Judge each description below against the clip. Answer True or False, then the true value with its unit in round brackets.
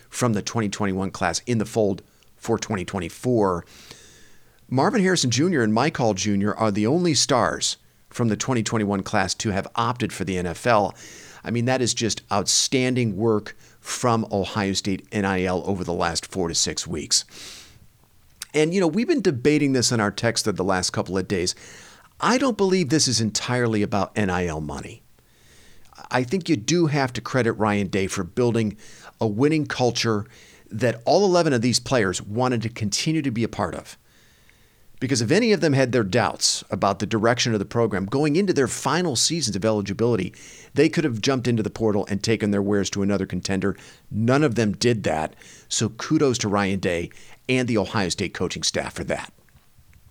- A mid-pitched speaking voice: False (110 Hz)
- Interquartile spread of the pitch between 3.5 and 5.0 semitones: True (4.2 semitones)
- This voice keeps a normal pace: True (185 wpm)